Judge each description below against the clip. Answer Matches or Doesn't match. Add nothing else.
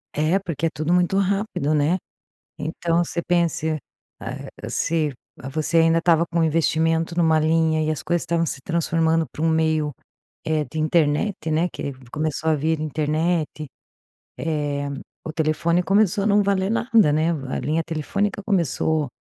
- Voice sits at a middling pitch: Matches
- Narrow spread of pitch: Matches